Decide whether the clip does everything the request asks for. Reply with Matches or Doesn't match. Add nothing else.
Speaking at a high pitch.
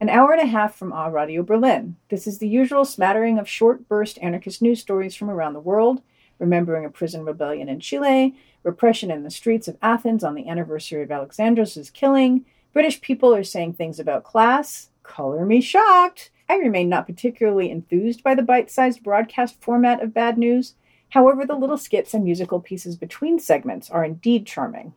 Matches